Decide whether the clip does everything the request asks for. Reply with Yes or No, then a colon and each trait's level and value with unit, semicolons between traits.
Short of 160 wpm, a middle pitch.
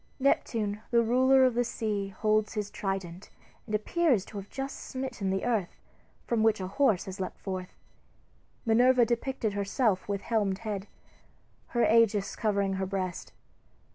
No: average, 150 wpm; high, 215 Hz